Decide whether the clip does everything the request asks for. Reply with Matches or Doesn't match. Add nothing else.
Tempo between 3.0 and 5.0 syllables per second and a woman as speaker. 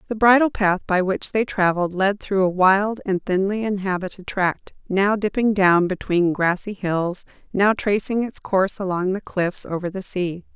Matches